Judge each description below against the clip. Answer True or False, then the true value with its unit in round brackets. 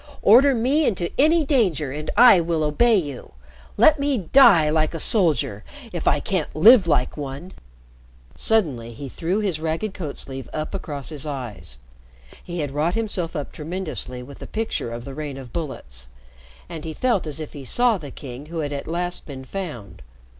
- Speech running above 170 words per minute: True (180 wpm)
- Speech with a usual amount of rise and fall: False (5.9 semitones)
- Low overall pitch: False (160 Hz)